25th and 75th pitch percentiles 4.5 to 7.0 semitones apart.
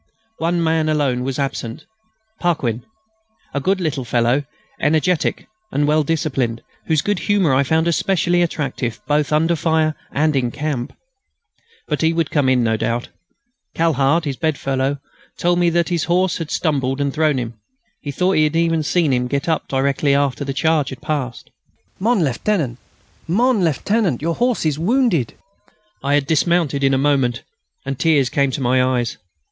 No: average, 3.7 semitones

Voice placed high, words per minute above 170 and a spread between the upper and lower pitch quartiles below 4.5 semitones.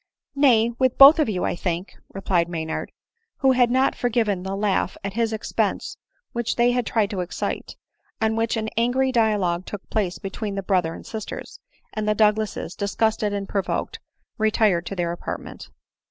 Yes: high, 215 Hz; average, 185 wpm; average, 3.4 semitones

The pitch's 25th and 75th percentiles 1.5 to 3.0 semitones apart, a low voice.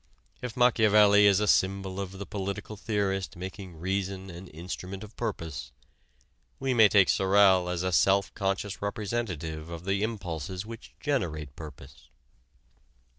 Yes: narrow, 2.5 semitones; very low, 95 Hz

